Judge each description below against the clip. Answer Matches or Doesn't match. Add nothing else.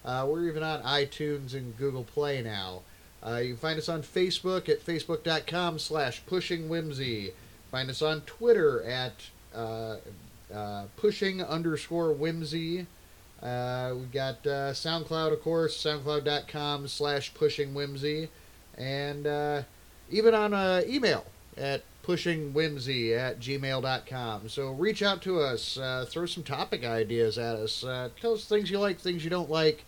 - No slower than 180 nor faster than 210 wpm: Doesn't match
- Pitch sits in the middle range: Matches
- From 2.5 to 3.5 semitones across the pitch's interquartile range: Doesn't match